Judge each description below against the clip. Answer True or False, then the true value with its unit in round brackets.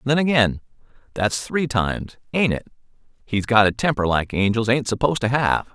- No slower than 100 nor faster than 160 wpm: True (155 wpm)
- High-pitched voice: False (120 Hz)